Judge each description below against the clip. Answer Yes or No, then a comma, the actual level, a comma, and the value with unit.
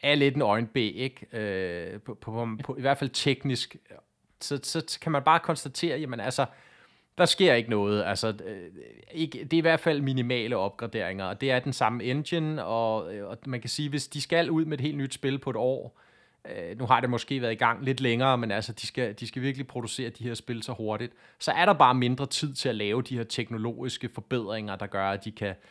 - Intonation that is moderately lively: Yes, average, 3.5 semitones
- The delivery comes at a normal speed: No, fast, 230 wpm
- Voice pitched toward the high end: No, low, 125 Hz